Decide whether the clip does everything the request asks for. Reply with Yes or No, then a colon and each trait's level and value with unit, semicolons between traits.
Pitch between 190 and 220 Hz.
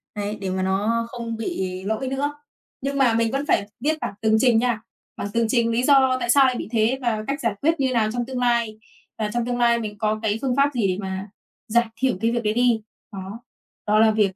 No: high, 230 Hz